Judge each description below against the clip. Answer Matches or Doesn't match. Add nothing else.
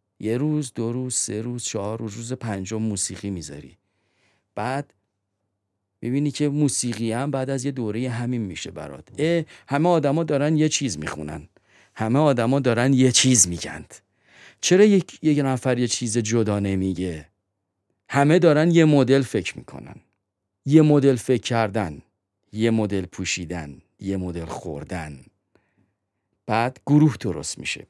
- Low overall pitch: Matches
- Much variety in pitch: Matches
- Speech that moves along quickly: Doesn't match